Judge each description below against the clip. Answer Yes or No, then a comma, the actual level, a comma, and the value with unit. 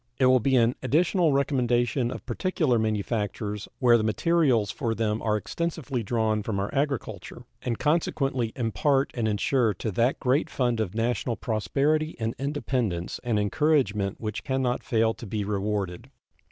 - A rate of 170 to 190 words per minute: No, average, 155 wpm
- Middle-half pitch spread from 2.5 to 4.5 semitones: Yes, average, 4.1 semitones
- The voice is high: No, low, 120 Hz